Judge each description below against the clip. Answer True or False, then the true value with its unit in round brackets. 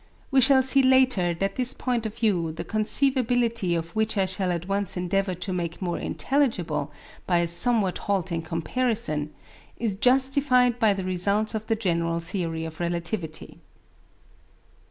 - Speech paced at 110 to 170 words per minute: True (155 wpm)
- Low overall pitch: False (195 Hz)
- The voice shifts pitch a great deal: True (5.7 semitones)